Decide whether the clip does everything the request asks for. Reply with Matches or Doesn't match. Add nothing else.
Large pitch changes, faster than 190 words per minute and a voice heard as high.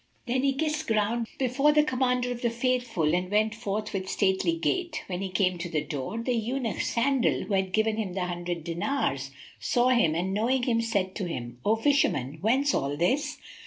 Matches